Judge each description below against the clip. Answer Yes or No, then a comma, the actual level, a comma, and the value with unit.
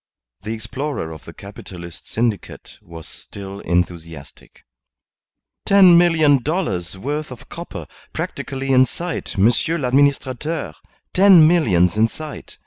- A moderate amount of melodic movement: No, wide, 8.6 semitones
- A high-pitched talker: No, low, 130 Hz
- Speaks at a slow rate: Yes, slow, 115 wpm